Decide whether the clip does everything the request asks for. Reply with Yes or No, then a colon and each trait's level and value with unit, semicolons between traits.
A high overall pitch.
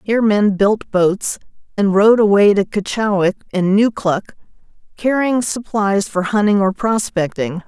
Yes: high, 205 Hz